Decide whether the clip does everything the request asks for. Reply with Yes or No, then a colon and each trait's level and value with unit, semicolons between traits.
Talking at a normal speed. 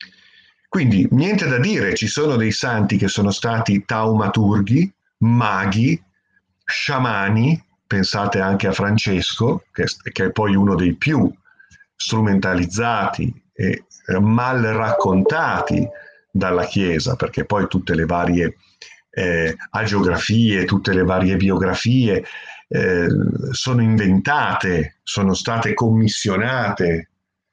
No: slow, 100 wpm